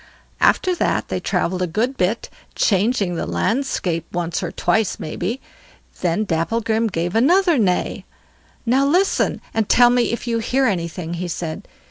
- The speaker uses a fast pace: No, average, 150 wpm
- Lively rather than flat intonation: Yes, wide, 5.8 semitones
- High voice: Yes, high, 215 Hz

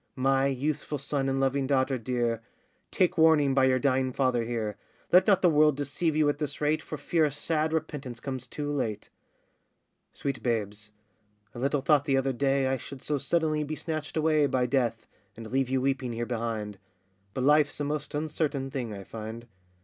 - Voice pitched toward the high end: No, low, 135 Hz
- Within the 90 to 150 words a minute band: No, average, 190 wpm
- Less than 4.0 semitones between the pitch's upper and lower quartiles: Yes, average, 3.1 semitones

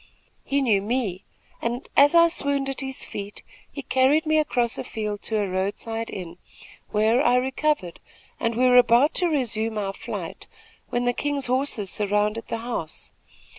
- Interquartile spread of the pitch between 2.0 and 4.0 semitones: No, average, 4.4 semitones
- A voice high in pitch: Yes, high, 240 Hz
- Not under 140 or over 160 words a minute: No, average, 170 wpm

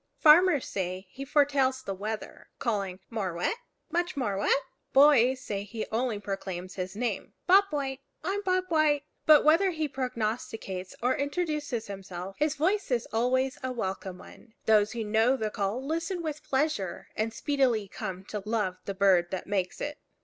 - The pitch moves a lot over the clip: Yes, wide, 6.7 semitones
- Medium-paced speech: Yes, average, 165 wpm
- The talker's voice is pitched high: Yes, high, 240 Hz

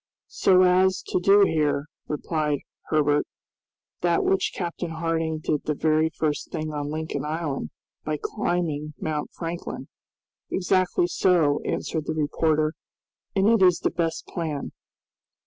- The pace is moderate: No, slow, 130 wpm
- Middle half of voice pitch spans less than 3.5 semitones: Yes, narrow, 2.5 semitones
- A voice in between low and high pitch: Yes, medium, 160 Hz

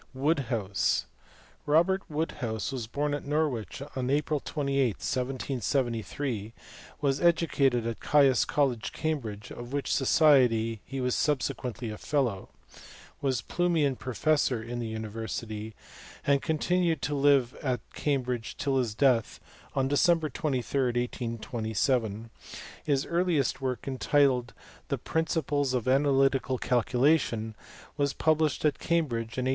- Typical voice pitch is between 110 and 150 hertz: Yes, low, 135 Hz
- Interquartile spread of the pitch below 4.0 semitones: Yes, average, 3.6 semitones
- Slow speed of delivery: Yes, slow, 120 wpm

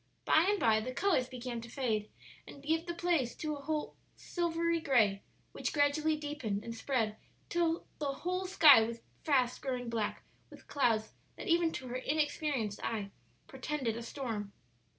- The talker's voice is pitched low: No, very high, 270 Hz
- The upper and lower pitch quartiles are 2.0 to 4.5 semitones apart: No, average, 5.3 semitones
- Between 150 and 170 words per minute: Yes, average, 155 wpm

